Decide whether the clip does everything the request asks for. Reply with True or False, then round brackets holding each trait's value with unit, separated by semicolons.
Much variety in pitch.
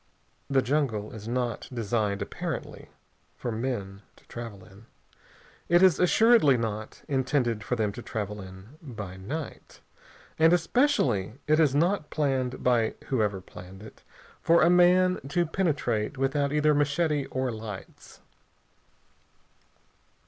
True (6.1 semitones)